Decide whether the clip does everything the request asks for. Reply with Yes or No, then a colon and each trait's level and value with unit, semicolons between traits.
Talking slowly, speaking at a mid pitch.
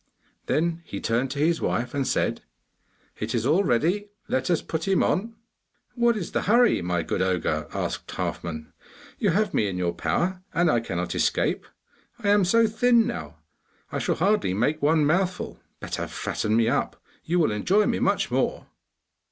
No: average, 175 wpm; medium, 160 Hz